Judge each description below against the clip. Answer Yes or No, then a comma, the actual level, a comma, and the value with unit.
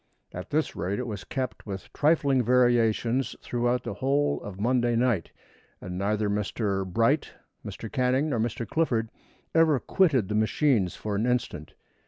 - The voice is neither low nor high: No, low, 120 Hz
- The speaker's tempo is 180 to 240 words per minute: No, average, 155 wpm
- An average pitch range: Yes, average, 3.9 semitones